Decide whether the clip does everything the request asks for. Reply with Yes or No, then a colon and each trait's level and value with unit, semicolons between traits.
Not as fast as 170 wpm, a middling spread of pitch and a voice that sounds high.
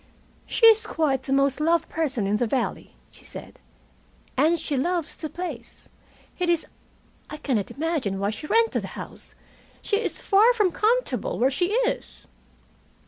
No: average, 160 wpm; wide, 5.8 semitones; very high, 315 Hz